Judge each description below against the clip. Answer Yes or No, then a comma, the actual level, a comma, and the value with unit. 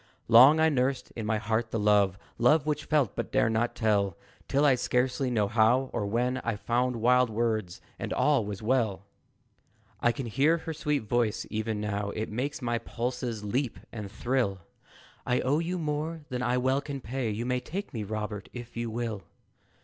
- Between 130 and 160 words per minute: No, average, 190 wpm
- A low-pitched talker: Yes, low, 120 Hz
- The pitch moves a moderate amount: Yes, average, 3.4 semitones